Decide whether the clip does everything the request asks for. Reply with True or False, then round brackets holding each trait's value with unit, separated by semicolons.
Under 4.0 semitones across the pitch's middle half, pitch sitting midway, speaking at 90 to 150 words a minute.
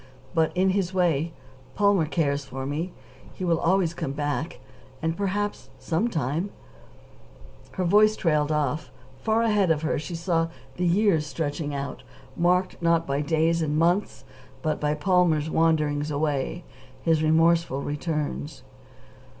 True (3.3 semitones; 160 Hz; 140 wpm)